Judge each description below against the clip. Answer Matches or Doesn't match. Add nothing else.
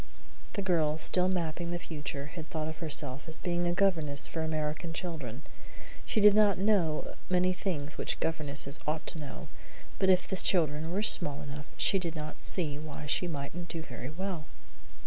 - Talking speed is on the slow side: Doesn't match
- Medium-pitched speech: Matches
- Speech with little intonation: Doesn't match